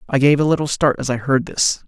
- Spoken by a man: Yes, male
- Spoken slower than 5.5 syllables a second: No, 6.1 syllables/s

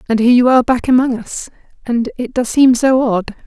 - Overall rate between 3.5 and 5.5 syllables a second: No, 5.7 syllables/s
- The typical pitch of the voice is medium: No, high, 245 Hz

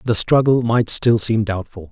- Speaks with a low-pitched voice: Yes, low, 110 Hz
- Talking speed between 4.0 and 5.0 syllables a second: Yes, 4.6 syllables/s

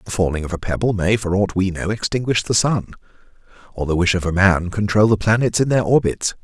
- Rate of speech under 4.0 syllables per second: No, 5.8 syllables/s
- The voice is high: No, low, 100 Hz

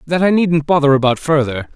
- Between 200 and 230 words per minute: Yes, fast, 205 wpm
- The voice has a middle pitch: Yes, medium, 150 Hz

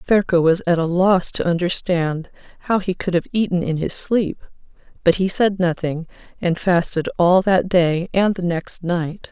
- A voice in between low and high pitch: Yes, medium, 175 Hz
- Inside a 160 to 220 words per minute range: Yes, average, 180 wpm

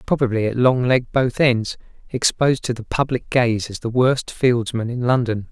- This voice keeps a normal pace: Yes, average, 185 wpm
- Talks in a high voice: No, low, 120 Hz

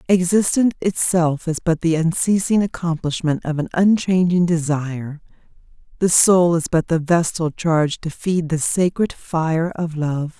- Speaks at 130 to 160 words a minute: Yes, average, 145 wpm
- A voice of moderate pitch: Yes, medium, 170 Hz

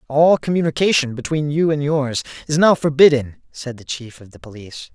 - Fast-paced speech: No, average, 180 wpm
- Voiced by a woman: No, male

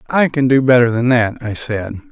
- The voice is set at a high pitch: No, low, 125 Hz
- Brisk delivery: Yes, fast, 225 wpm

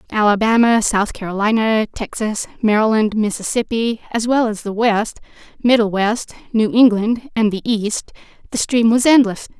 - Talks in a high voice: Yes, high, 220 Hz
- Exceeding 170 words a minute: No, average, 140 wpm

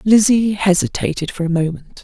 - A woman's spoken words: Yes, female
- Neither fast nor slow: Yes, average, 145 wpm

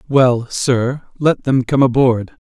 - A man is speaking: Yes, male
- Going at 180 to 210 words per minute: No, average, 145 wpm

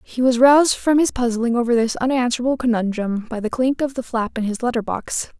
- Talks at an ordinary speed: No, fast, 225 wpm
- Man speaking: No, female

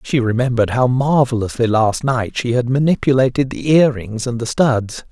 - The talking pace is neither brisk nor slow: Yes, average, 175 wpm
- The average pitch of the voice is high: No, low, 125 Hz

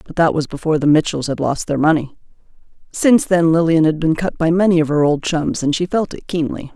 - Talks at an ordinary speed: No, fast, 240 wpm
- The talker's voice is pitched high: No, medium, 160 Hz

